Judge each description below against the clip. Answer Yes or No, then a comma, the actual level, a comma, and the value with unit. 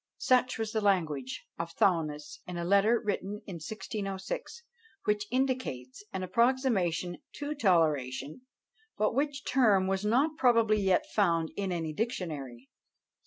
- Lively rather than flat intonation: Yes, wide, 5.7 semitones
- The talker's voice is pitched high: Yes, high, 195 Hz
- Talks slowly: Yes, slow, 130 wpm